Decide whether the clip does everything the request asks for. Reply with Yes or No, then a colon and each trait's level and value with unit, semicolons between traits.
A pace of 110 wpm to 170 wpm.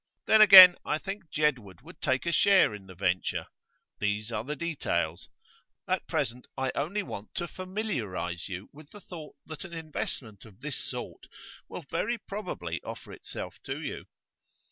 Yes: average, 160 wpm